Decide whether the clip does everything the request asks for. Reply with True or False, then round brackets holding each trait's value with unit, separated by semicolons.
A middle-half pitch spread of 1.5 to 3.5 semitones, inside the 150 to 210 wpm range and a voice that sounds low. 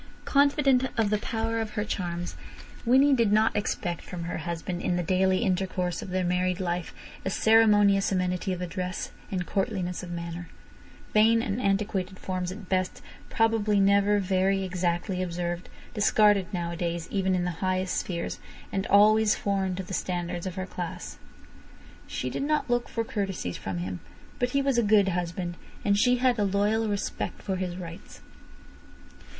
False (3.0 semitones; 165 wpm; 190 Hz)